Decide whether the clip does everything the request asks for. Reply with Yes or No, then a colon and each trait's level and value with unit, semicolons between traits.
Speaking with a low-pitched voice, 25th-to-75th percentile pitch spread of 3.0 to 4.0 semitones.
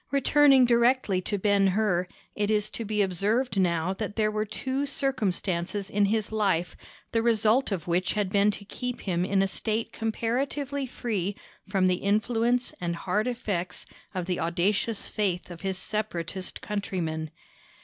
No: high, 205 Hz; average, 3.6 semitones